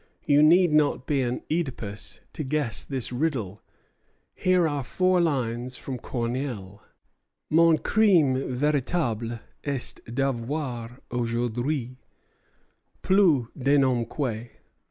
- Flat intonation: No, average, 4.2 semitones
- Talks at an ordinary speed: No, slow, 105 wpm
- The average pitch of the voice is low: Yes, low, 130 Hz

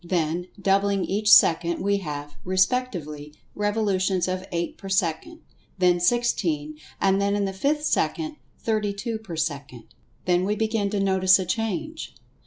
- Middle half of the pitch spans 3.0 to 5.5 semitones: Yes, average, 3.4 semitones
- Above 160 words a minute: No, average, 150 wpm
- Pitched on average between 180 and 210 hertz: Yes, high, 190 Hz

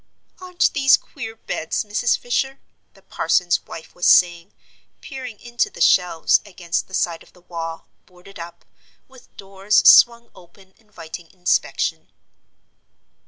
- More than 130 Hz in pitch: Yes, high, 190 Hz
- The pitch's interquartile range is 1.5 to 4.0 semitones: No, average, 5.3 semitones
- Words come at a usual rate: No, slow, 130 wpm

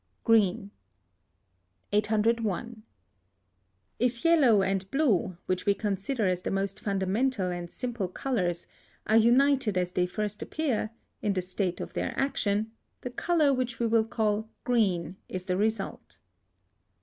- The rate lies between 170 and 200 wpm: No, slow, 135 wpm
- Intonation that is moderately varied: Yes, average, 3.9 semitones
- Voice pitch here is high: Yes, high, 210 Hz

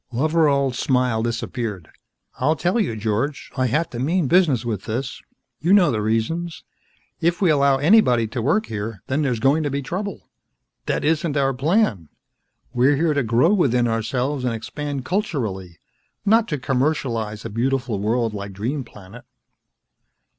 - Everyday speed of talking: Yes, average, 155 wpm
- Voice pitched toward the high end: No, low, 130 Hz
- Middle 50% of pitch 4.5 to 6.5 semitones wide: Yes, wide, 5.4 semitones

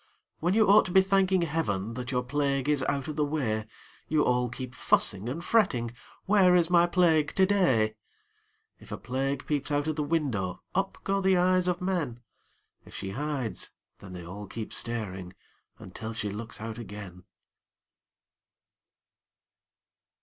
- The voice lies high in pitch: No, medium, 140 Hz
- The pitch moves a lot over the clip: Yes, wide, 7.7 semitones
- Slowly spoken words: No, average, 160 wpm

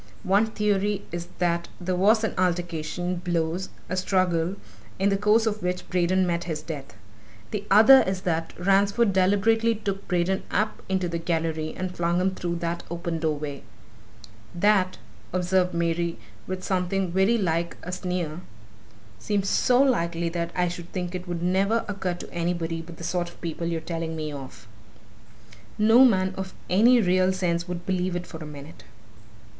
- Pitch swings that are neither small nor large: No, narrow, 2.3 semitones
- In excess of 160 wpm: Yes, average, 170 wpm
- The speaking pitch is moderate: Yes, medium, 180 Hz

